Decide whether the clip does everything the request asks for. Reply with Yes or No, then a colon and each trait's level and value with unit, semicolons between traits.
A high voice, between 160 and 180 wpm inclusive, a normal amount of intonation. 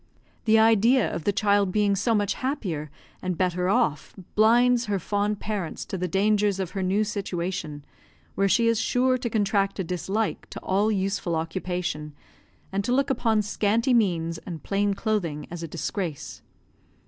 Yes: high, 200 Hz; average, 165 wpm; average, 3.3 semitones